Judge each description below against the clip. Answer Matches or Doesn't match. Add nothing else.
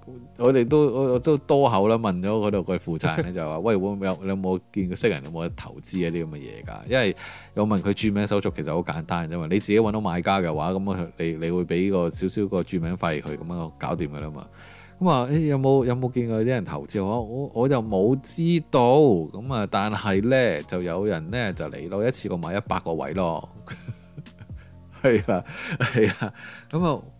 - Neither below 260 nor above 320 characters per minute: Matches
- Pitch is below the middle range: Matches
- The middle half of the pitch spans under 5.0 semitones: Doesn't match